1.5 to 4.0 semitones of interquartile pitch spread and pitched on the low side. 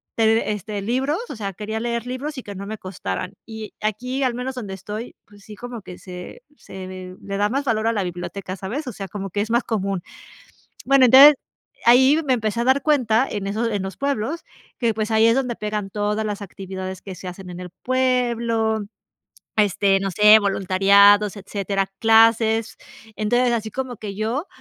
No: average, 3.4 semitones; high, 215 Hz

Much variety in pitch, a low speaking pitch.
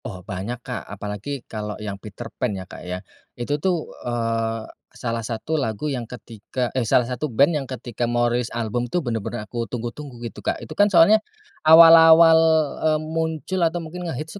Yes: wide, 5.9 semitones; low, 120 Hz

